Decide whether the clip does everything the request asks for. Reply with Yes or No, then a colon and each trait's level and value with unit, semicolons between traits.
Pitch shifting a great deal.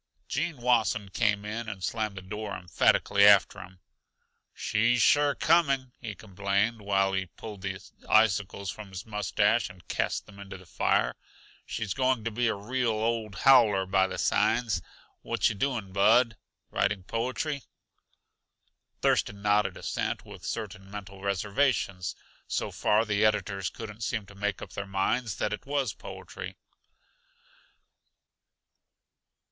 No: average, 2.9 semitones